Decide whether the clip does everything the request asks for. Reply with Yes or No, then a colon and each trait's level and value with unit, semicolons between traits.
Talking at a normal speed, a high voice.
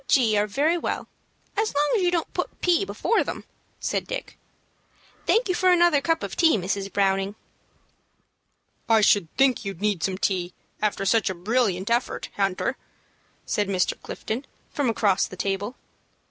Yes: average, 160 wpm; high, 215 Hz